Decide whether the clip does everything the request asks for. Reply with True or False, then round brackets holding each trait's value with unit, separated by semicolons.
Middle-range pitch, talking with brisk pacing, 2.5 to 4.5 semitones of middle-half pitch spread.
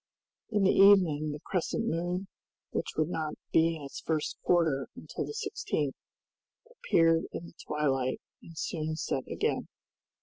False (165 Hz; 145 wpm; 3.0 semitones)